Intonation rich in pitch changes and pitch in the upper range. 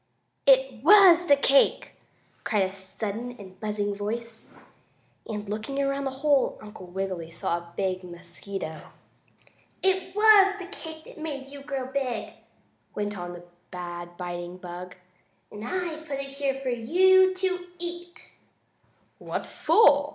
Yes: wide, 8.6 semitones; very high, 255 Hz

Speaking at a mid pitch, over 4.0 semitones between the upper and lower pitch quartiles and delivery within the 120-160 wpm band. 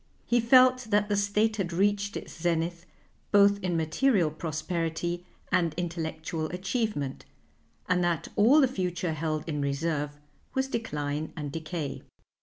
Yes: medium, 175 Hz; average, 4.5 semitones; slow, 135 wpm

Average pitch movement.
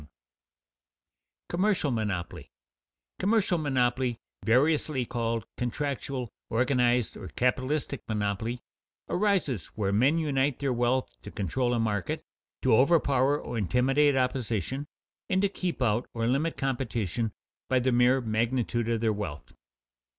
Yes: average, 3.5 semitones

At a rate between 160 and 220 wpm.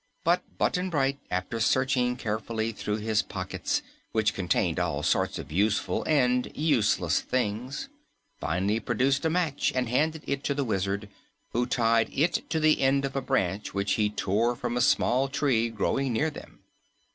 Yes: average, 165 wpm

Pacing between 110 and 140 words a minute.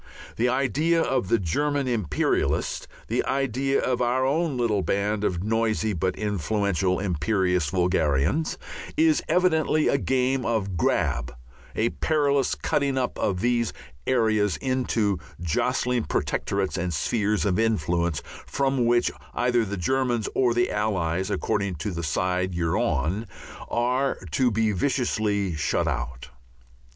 Yes: slow, 135 wpm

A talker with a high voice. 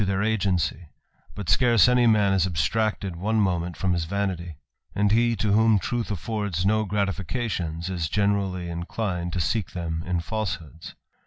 No: very low, 95 Hz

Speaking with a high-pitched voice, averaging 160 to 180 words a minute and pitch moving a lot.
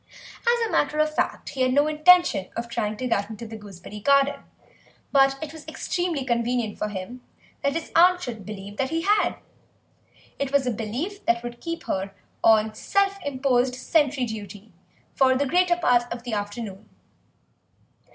Yes: very high, 255 Hz; average, 170 wpm; wide, 5.9 semitones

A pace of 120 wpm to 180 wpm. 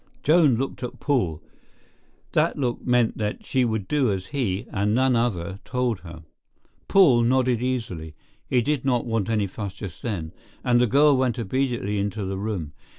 Yes: average, 160 wpm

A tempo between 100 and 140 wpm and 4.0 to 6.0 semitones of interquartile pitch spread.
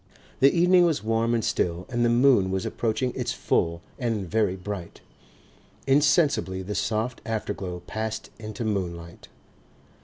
Yes: slow, 135 wpm; average, 4.3 semitones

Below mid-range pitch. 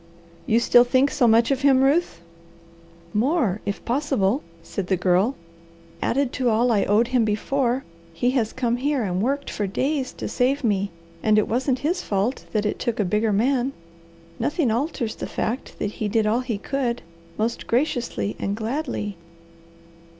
No: high, 235 Hz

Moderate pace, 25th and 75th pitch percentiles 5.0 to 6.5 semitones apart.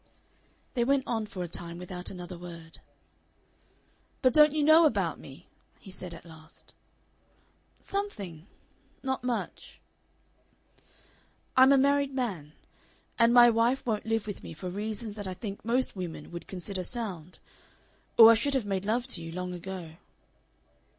Yes: average, 150 wpm; wide, 5.6 semitones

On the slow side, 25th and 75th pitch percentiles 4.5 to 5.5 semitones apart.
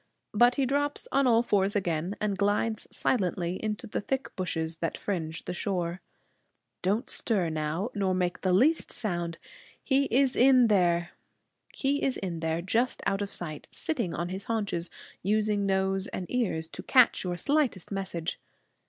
No: average, 150 wpm; average, 5.2 semitones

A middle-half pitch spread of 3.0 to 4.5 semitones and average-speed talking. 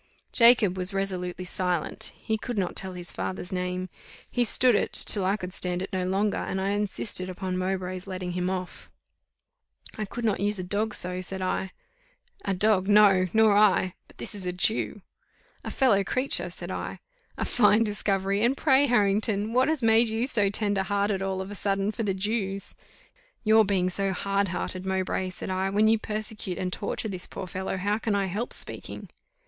No: narrow, 2.5 semitones; average, 190 wpm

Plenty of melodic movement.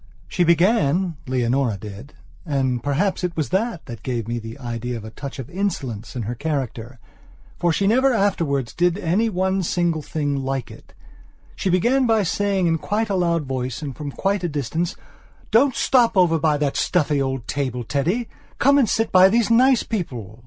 Yes: wide, 6.8 semitones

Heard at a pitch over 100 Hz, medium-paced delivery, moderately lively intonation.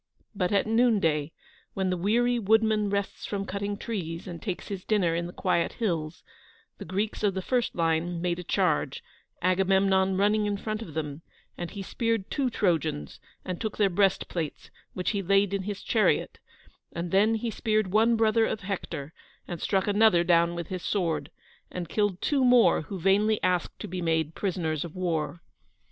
Yes: high, 190 Hz; average, 180 wpm; average, 3.6 semitones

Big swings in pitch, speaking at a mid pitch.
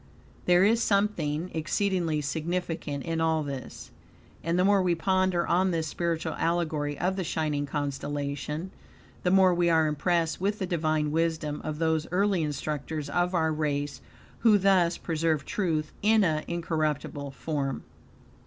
No: average, 3.0 semitones; medium, 165 Hz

